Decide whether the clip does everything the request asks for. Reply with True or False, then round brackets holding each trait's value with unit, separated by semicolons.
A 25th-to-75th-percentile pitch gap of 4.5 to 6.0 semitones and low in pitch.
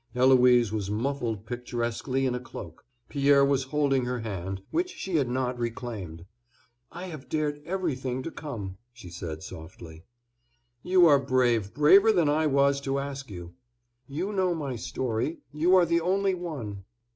True (5.1 semitones; 130 Hz)